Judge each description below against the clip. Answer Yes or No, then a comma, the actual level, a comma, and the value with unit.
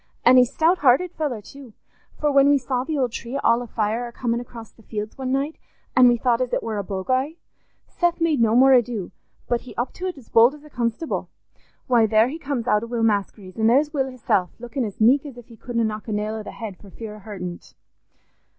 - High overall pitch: Yes, high, 240 Hz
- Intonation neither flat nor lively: Yes, average, 3.5 semitones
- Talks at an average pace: No, fast, 240 wpm